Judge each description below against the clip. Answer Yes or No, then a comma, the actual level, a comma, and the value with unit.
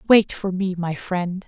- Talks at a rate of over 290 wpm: No, fast, 205 wpm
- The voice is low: No, medium, 185 Hz